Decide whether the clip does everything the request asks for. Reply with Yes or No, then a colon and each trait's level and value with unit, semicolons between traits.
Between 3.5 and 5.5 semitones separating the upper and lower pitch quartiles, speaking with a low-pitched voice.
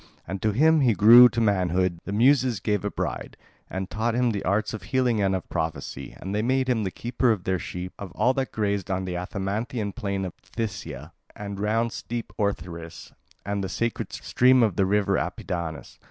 Yes: average, 3.9 semitones; low, 105 Hz